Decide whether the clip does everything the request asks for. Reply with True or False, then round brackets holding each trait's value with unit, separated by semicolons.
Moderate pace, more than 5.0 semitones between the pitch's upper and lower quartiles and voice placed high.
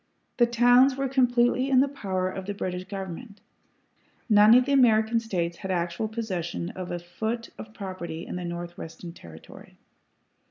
True (160 wpm; 5.4 semitones; 205 Hz)